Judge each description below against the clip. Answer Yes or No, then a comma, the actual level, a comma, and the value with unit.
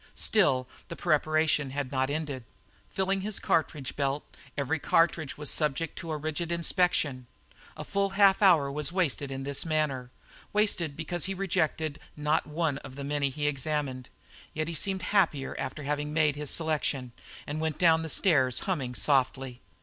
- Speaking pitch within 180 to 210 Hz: No, medium, 150 Hz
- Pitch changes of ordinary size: Yes, average, 3.3 semitones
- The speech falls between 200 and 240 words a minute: No, average, 165 wpm